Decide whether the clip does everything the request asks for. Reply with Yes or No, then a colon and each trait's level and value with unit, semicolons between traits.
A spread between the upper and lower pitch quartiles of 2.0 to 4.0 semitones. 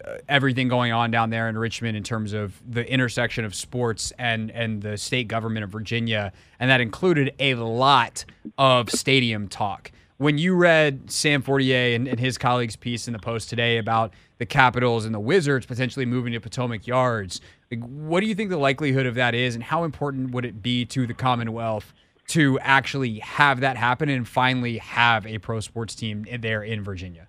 Yes: average, 2.8 semitones